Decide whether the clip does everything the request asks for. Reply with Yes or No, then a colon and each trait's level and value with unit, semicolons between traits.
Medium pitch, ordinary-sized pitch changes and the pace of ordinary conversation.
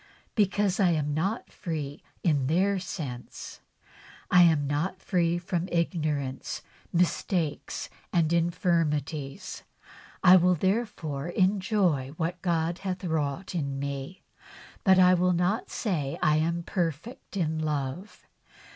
No: medium, 170 Hz; average, 3.5 semitones; slow, 120 wpm